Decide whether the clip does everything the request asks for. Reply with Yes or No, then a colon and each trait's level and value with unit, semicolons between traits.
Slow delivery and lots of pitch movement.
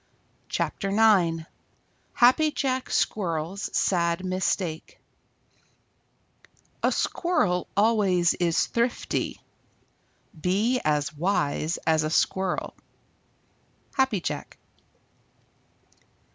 No: slow, 75 wpm; average, 4.9 semitones